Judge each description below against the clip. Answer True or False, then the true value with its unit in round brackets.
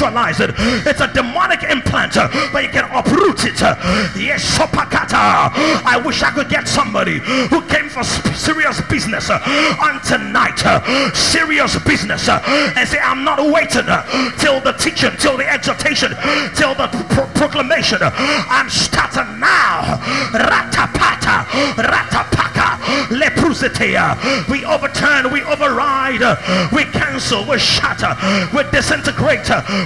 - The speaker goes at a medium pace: False (110 wpm)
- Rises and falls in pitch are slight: True (1.9 semitones)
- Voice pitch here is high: True (290 Hz)